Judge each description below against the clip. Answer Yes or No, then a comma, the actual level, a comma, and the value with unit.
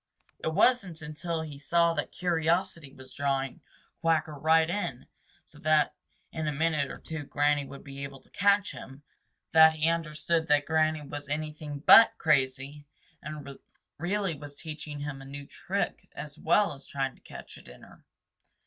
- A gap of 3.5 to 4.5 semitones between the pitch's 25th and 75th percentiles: No, narrow, 2.5 semitones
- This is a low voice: No, medium, 150 Hz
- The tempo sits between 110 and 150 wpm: No, average, 165 wpm